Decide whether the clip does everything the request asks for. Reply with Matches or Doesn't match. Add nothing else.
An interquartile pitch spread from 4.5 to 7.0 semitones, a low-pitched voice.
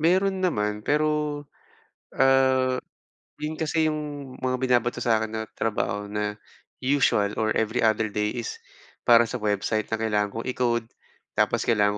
Matches